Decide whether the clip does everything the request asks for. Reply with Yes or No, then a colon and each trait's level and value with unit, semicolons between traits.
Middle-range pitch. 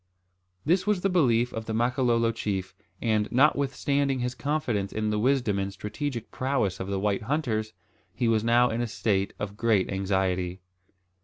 No: low, 115 Hz